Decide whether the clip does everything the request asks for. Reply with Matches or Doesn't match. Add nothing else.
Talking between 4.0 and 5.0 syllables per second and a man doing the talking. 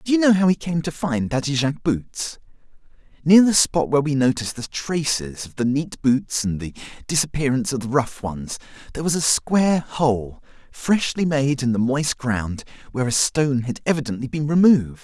Doesn't match